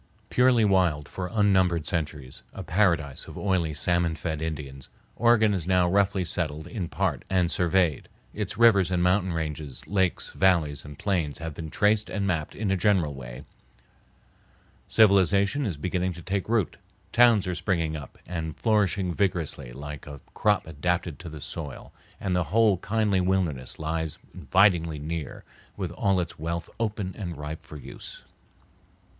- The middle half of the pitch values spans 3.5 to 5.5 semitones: Yes, average, 3.9 semitones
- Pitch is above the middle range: No, very low, 90 Hz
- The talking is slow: No, average, 155 wpm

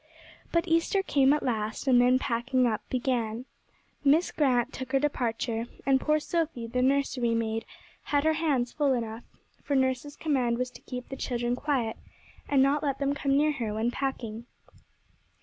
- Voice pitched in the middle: No, very high, 260 Hz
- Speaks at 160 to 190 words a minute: Yes, average, 170 wpm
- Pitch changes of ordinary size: Yes, average, 3.1 semitones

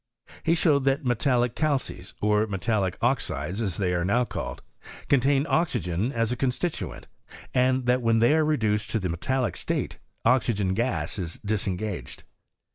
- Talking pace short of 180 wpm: Yes, average, 155 wpm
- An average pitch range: Yes, average, 4.9 semitones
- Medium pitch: No, low, 115 Hz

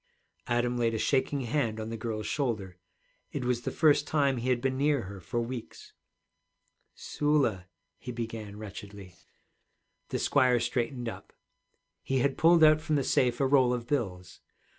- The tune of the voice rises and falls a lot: No, average, 3.7 semitones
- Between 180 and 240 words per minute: No, average, 160 wpm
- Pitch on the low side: Yes, low, 120 Hz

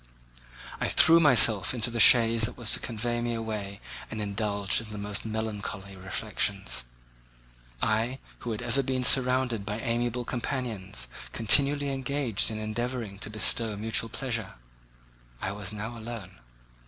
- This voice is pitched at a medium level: No, low, 110 Hz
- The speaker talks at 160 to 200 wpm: No, average, 140 wpm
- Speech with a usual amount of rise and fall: Yes, average, 3.0 semitones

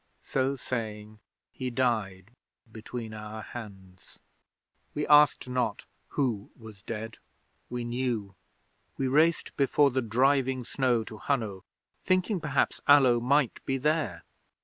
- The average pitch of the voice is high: No, low, 125 Hz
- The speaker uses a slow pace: Yes, slow, 120 wpm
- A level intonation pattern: No, average, 4.0 semitones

